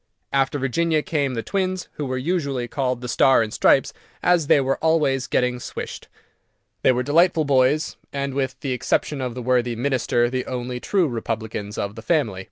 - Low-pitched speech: Yes, low, 130 Hz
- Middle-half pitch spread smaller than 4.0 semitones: Yes, average, 3.1 semitones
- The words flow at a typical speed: Yes, average, 180 wpm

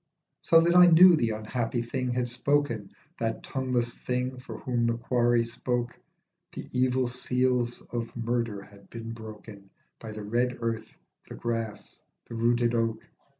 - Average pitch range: No, narrow, 1.7 semitones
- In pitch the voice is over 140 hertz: No, low, 120 Hz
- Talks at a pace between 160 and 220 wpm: No, average, 150 wpm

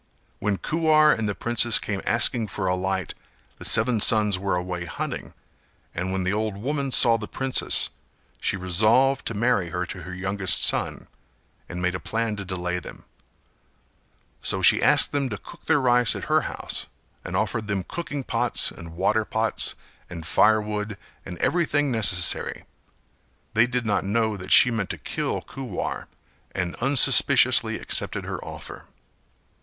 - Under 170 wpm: Yes, average, 160 wpm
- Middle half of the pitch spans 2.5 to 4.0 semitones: No, average, 4.5 semitones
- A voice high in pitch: No, low, 105 Hz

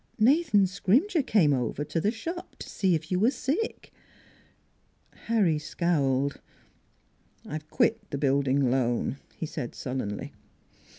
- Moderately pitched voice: Yes, medium, 165 Hz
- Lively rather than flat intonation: Yes, wide, 8.3 semitones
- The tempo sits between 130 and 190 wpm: Yes, slow, 135 wpm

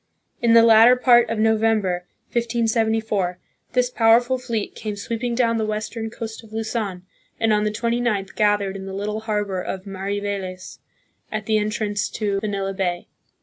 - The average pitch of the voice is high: Yes, high, 215 Hz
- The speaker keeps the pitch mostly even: Yes, narrow, 2.3 semitones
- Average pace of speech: Yes, average, 155 wpm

